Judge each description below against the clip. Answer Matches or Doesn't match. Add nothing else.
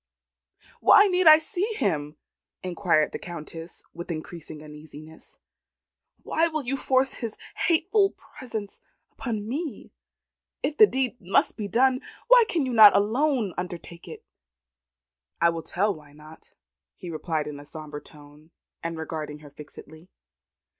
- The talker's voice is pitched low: Doesn't match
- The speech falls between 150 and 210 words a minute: Doesn't match